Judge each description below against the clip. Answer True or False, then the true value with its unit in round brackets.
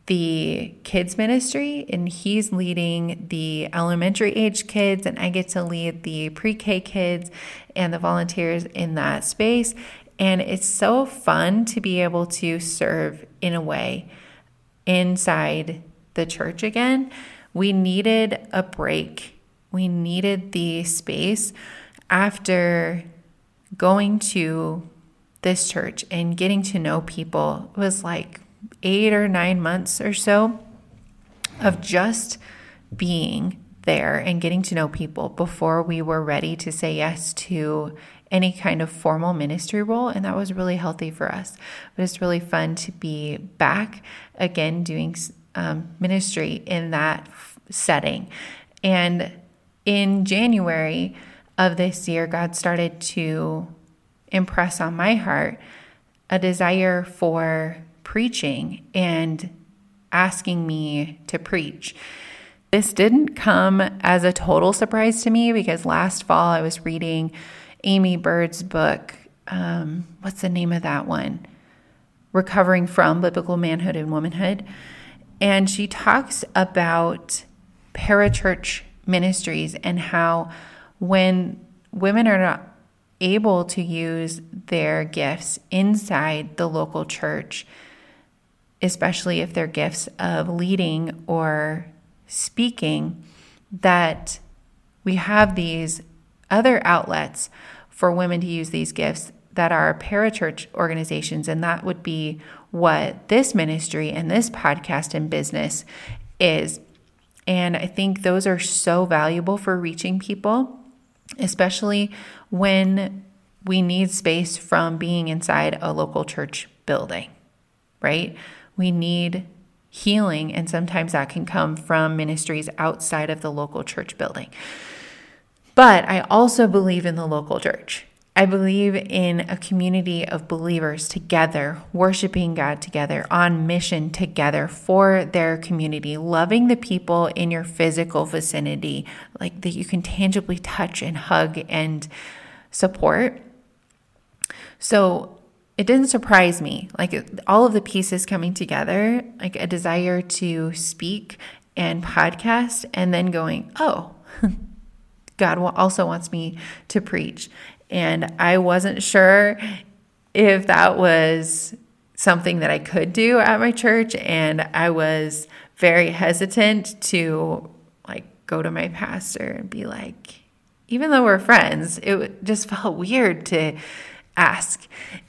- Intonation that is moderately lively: True (3.1 semitones)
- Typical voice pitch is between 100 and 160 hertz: False (180 Hz)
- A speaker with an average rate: False (125 wpm)